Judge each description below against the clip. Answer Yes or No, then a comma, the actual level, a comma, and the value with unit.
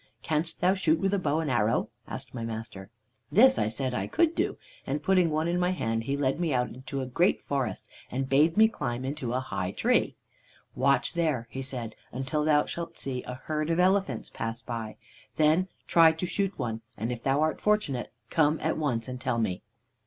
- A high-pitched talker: No, medium, 140 Hz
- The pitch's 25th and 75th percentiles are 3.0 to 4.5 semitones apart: No, average, 5.3 semitones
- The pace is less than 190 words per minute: No, fast, 205 wpm